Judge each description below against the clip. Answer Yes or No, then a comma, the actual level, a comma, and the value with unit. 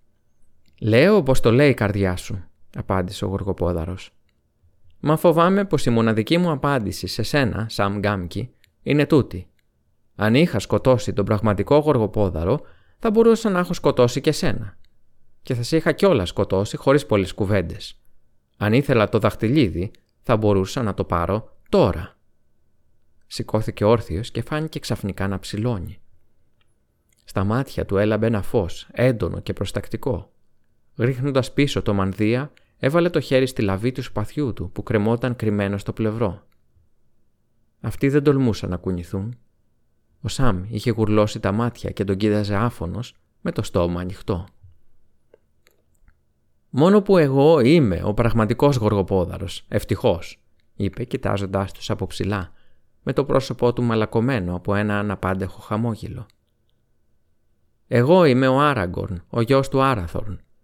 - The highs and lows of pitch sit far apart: No, average, 4.8 semitones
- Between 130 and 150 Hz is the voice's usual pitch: No, low, 110 Hz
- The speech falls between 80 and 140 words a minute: Yes, average, 135 wpm